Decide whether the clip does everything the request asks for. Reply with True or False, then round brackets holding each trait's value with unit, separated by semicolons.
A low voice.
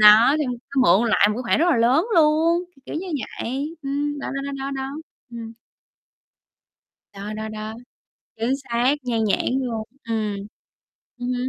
False (250 Hz)